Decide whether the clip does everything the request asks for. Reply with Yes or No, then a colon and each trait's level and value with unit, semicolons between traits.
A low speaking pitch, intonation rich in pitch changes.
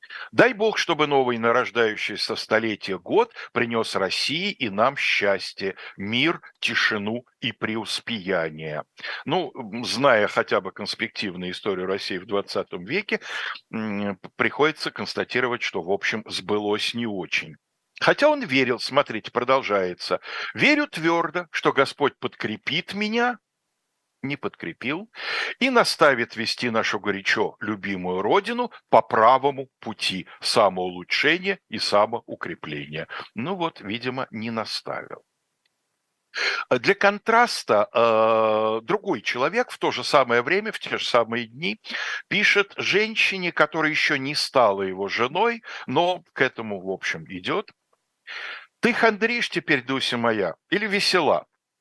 Yes: low, 125 Hz; wide, 9.0 semitones